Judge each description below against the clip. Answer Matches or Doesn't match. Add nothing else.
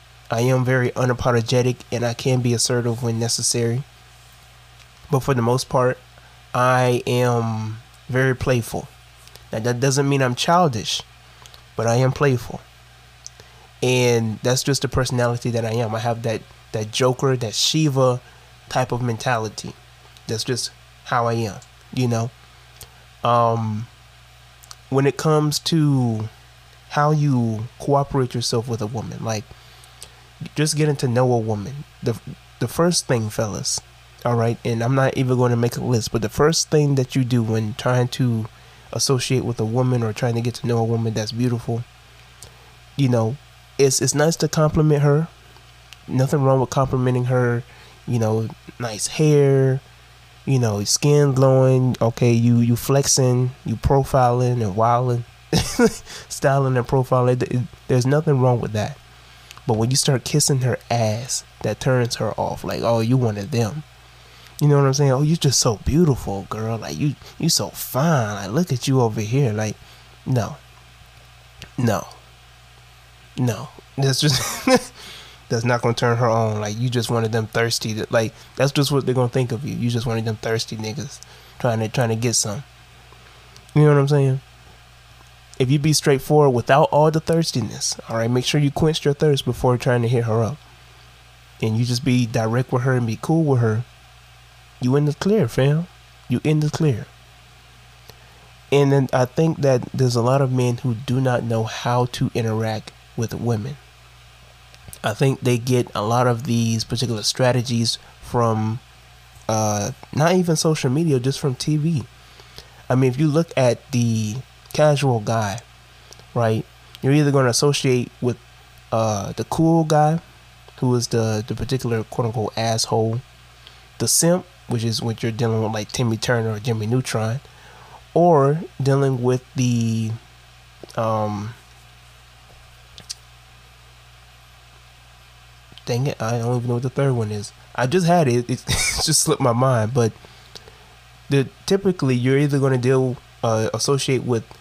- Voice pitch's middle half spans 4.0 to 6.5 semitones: Doesn't match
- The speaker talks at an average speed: Matches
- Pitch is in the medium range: Doesn't match